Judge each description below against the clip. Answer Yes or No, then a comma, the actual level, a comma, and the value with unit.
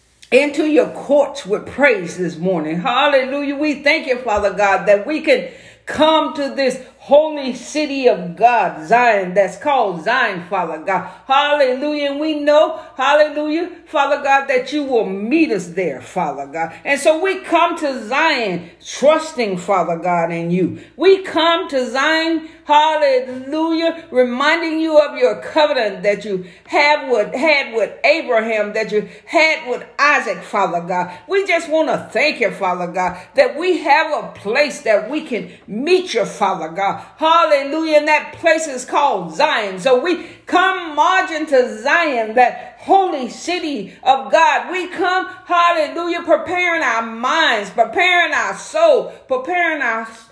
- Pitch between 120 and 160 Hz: No, very high, 290 Hz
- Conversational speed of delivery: Yes, average, 155 wpm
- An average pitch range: No, wide, 6.2 semitones